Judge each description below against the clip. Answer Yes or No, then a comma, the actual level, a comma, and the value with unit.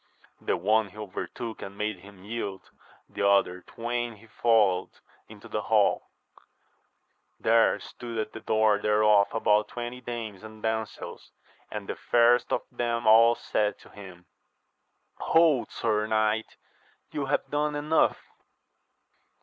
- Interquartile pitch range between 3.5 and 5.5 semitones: No, narrow, 2.4 semitones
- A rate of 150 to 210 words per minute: No, slow, 135 wpm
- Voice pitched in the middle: No, low, 110 Hz